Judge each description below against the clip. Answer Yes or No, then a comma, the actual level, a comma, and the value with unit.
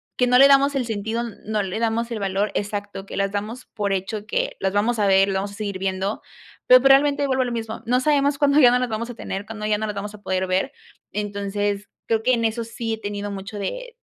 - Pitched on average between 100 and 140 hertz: No, high, 215 Hz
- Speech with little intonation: No, average, 3.4 semitones